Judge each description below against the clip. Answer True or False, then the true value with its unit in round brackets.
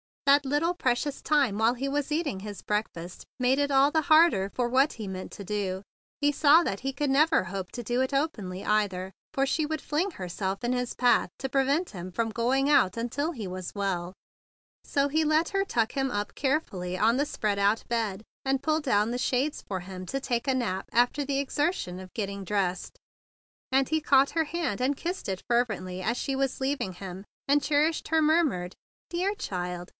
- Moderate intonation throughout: False (6.5 semitones)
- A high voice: True (250 Hz)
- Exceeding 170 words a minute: True (200 wpm)